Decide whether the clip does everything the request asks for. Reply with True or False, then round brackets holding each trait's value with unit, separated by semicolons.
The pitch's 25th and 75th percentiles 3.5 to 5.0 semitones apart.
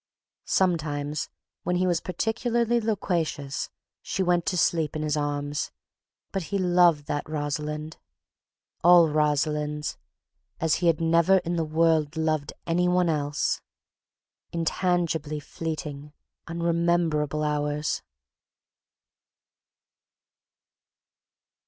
False (2.7 semitones)